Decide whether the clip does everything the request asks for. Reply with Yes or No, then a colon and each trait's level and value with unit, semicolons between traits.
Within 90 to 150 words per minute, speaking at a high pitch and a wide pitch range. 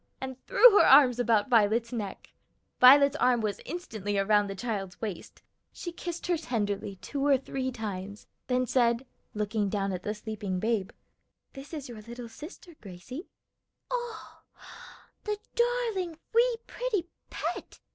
Yes: average, 145 wpm; high, 240 Hz; wide, 6.9 semitones